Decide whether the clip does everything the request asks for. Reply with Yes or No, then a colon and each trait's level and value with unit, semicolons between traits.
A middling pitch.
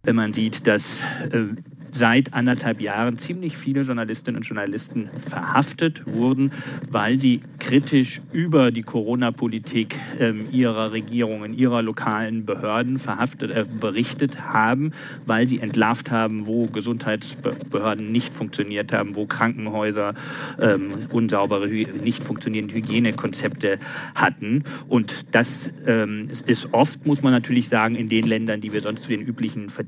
No: low, 115 Hz